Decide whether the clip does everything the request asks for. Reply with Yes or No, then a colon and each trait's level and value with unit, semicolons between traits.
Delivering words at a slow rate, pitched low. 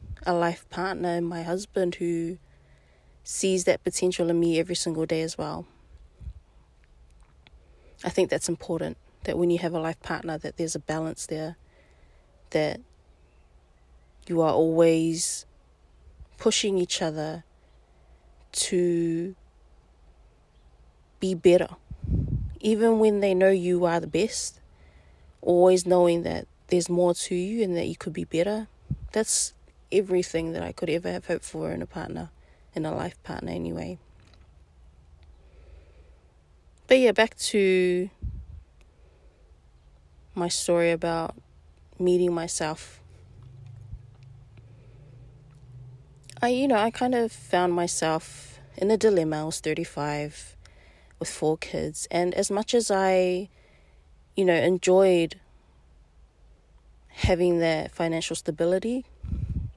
No: slow, 120 wpm; medium, 150 Hz